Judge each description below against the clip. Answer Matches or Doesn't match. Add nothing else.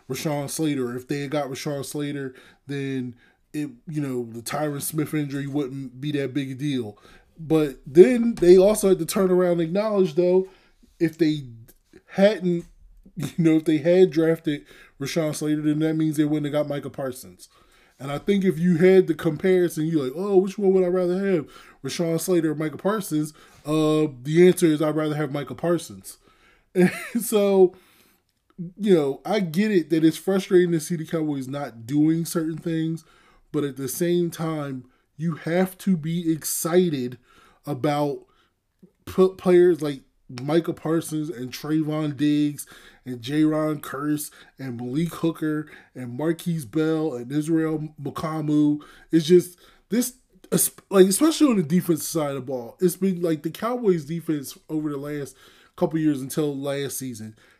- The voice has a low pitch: Doesn't match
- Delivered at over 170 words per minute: Doesn't match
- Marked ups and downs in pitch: Doesn't match